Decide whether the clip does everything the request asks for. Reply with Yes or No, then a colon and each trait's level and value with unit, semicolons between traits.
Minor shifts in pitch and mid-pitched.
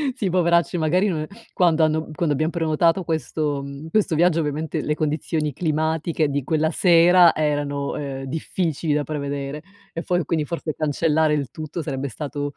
Yes: narrow, 2.3 semitones; medium, 155 Hz